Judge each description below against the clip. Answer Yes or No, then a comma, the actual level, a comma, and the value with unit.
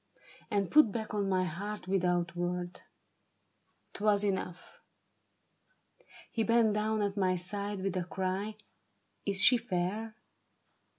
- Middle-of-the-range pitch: No, high, 195 Hz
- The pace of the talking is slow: Yes, slow, 125 wpm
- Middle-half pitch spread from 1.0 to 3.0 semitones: Yes, narrow, 2.5 semitones